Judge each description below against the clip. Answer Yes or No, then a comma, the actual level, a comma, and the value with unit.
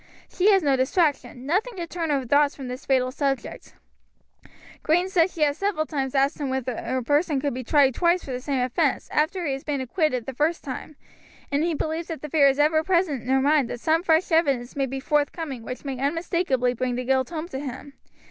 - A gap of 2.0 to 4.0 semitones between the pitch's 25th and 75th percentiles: Yes, average, 3.7 semitones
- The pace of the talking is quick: Yes, fast, 225 wpm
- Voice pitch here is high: Yes, very high, 285 Hz